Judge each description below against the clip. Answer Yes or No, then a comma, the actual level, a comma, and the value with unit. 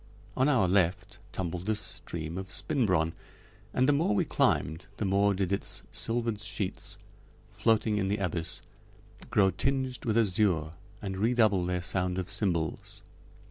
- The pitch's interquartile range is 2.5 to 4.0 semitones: Yes, average, 3.4 semitones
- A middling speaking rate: Yes, average, 145 wpm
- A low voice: Yes, low, 100 Hz